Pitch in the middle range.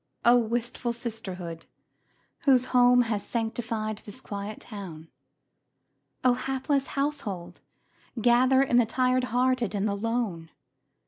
No: high, 235 Hz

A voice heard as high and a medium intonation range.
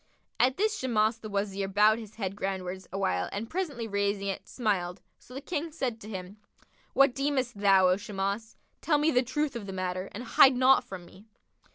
Yes: high, 215 Hz; average, 4.8 semitones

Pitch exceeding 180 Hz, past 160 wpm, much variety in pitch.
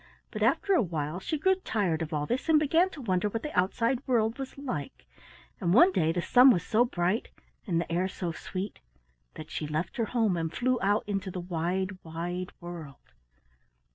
Yes: high, 190 Hz; average, 200 wpm; wide, 6.1 semitones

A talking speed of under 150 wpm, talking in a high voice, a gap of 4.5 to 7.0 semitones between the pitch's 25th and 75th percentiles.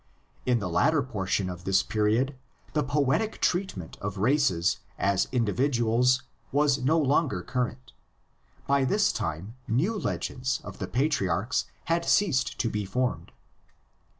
No: slow, 135 wpm; low, 125 Hz; wide, 5.6 semitones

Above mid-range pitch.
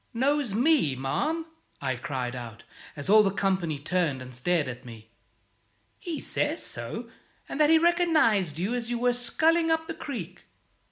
Yes: high, 200 Hz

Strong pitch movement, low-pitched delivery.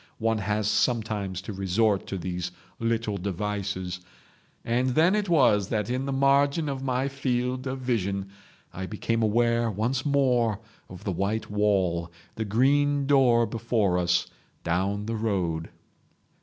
No: average, 4.6 semitones; low, 110 Hz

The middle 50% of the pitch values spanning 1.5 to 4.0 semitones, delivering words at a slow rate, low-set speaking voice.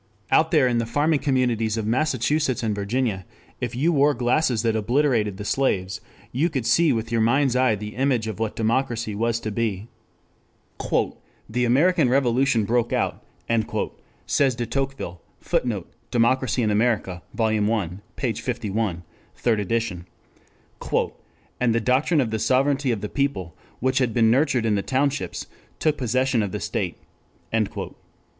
No: average, 3.4 semitones; average, 150 wpm; low, 120 Hz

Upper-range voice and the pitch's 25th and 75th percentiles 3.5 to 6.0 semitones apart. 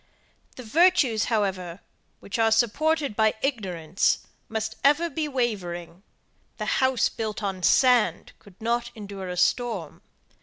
Yes: high, 220 Hz; average, 4.9 semitones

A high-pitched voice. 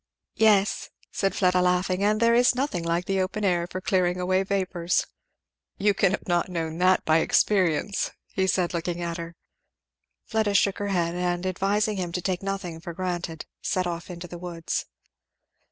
No: medium, 180 Hz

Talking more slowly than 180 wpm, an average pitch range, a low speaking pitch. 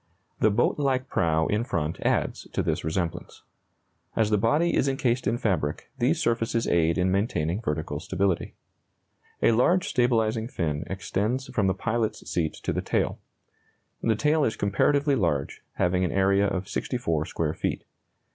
No: average, 155 wpm; wide, 5.8 semitones; low, 105 Hz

